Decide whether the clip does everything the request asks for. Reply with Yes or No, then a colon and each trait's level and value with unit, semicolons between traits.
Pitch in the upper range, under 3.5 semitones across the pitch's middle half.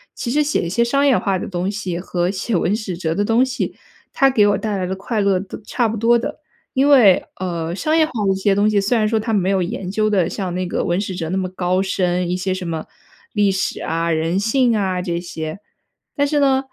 No: high, 195 Hz; average, 3.9 semitones